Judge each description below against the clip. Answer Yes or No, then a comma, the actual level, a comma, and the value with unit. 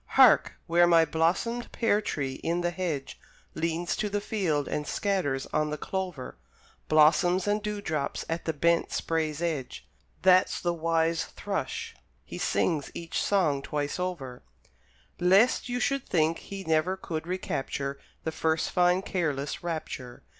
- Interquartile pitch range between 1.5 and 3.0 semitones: No, average, 3.4 semitones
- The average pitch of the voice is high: No, medium, 165 Hz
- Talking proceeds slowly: No, average, 145 wpm